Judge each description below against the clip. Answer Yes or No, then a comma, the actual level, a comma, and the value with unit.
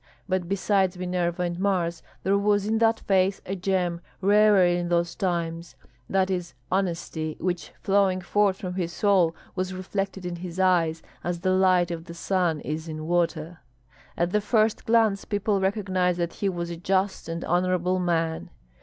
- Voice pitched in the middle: Yes, medium, 180 Hz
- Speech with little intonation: Yes, narrow, 2.1 semitones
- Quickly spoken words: No, average, 170 wpm